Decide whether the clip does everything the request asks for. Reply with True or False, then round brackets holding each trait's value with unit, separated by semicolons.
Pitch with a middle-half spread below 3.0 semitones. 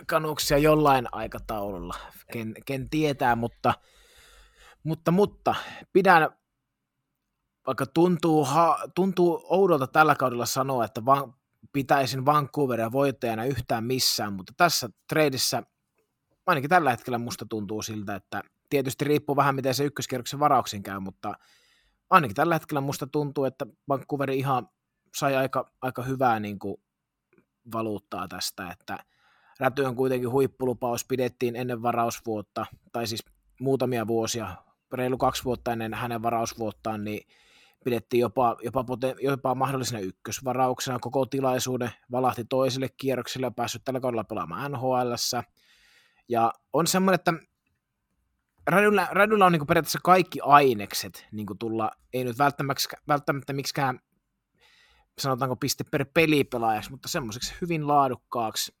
False (3.7 semitones)